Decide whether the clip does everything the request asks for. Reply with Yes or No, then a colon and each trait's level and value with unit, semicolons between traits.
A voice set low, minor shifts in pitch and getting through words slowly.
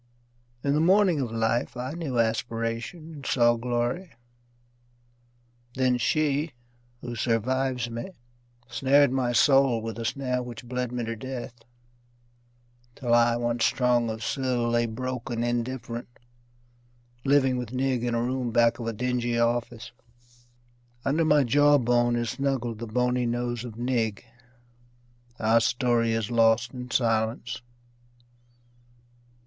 Yes: low, 120 Hz; narrow, 2.0 semitones; slow, 130 wpm